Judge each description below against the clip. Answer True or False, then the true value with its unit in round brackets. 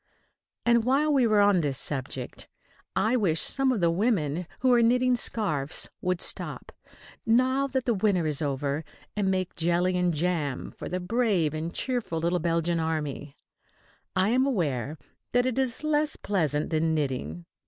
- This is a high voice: False (180 Hz)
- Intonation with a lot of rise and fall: True (7.3 semitones)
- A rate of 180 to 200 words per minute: False (160 wpm)